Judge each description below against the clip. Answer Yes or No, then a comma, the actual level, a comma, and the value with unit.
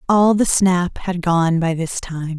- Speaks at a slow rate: No, average, 200 wpm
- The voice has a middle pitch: Yes, medium, 175 Hz